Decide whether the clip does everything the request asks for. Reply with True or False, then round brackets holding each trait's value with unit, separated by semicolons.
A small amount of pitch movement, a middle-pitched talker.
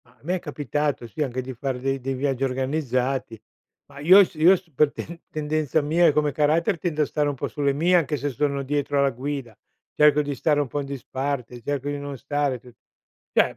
True (2.2 semitones; 145 Hz)